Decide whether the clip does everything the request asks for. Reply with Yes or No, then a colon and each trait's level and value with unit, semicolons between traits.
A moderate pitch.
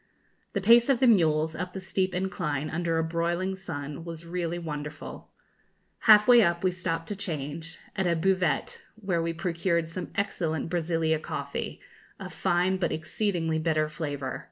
Yes: medium, 170 Hz